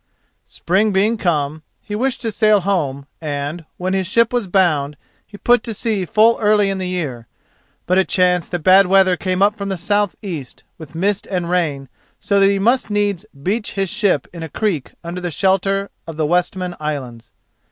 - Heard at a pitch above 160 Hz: Yes, medium, 185 Hz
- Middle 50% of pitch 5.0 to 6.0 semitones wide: No, average, 3.8 semitones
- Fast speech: No, average, 185 wpm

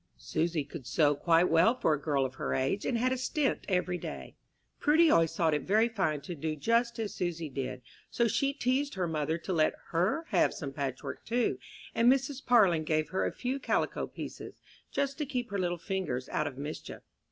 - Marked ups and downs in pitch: Yes, wide, 7.6 semitones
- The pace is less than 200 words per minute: No, fast, 205 wpm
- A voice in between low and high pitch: Yes, medium, 175 Hz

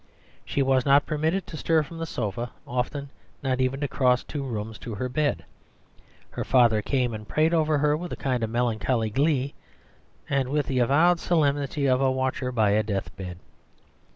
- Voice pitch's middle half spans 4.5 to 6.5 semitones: No, average, 3.5 semitones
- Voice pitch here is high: No, low, 130 Hz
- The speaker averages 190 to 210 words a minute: No, average, 180 wpm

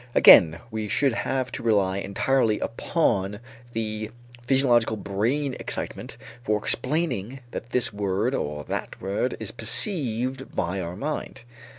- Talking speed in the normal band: No, slow, 125 wpm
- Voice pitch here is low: Yes, low, 115 Hz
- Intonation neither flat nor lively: Yes, average, 4.6 semitones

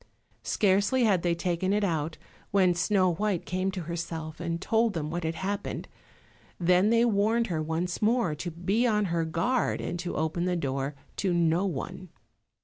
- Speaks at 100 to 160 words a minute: No, average, 175 wpm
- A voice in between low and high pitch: Yes, medium, 180 Hz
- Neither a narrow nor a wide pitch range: Yes, average, 3.3 semitones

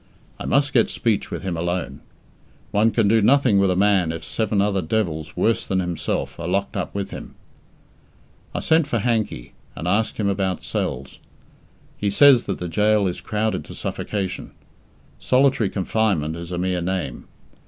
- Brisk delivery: No, average, 170 wpm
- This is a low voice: Yes, low, 100 Hz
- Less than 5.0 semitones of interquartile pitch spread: Yes, average, 3.8 semitones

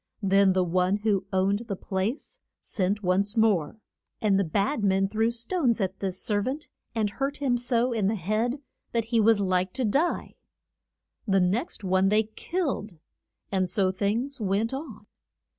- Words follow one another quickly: No, average, 165 wpm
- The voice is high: Yes, high, 210 Hz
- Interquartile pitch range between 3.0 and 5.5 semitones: Yes, average, 3.5 semitones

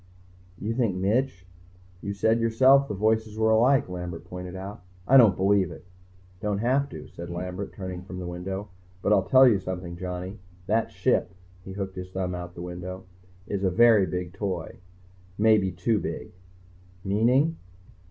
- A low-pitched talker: Yes, very low, 95 Hz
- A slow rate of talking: No, average, 175 wpm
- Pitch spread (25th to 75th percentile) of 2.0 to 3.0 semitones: No, average, 3.4 semitones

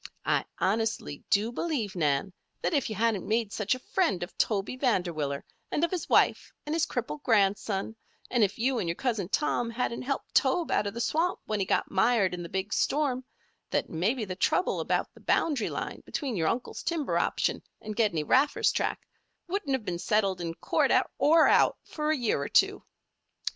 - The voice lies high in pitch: Yes, high, 225 Hz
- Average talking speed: Yes, average, 195 wpm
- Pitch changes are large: Yes, wide, 5.8 semitones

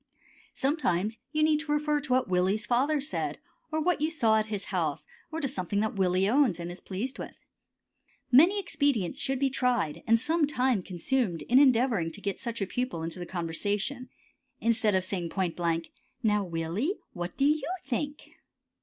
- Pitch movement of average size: No, wide, 7.2 semitones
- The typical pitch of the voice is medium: No, high, 230 Hz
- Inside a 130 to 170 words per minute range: No, average, 180 wpm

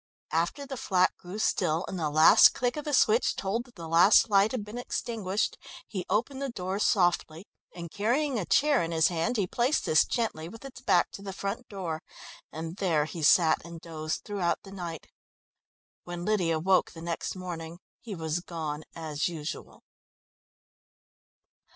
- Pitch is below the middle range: No, medium, 185 Hz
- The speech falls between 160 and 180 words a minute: Yes, average, 175 wpm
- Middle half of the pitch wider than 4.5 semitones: Yes, average, 4.9 semitones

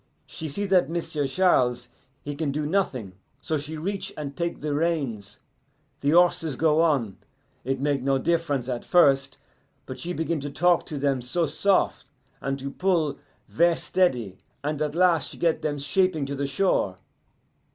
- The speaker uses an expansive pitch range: No, average, 3.7 semitones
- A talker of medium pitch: Yes, medium, 150 Hz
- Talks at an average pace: Yes, average, 170 wpm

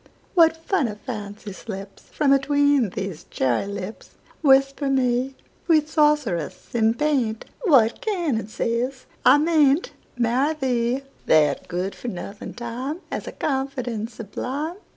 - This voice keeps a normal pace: No, slow, 100 wpm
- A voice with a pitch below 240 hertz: No, very high, 255 Hz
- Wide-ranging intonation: No, average, 4.8 semitones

